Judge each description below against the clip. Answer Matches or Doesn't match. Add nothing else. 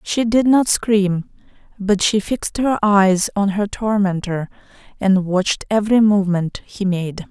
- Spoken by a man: Doesn't match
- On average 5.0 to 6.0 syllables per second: Doesn't match